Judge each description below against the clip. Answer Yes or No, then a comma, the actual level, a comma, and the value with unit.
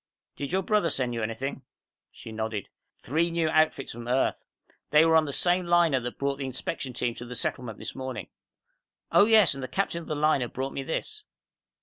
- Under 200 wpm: No, fast, 205 wpm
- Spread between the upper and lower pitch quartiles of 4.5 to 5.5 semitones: Yes, average, 5.2 semitones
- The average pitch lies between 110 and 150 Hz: Yes, medium, 140 Hz